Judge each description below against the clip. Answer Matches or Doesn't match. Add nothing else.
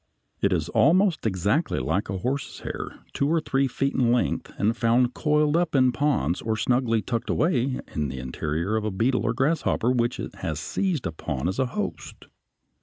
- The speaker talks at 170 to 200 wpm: Matches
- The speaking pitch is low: Matches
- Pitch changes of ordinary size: Doesn't match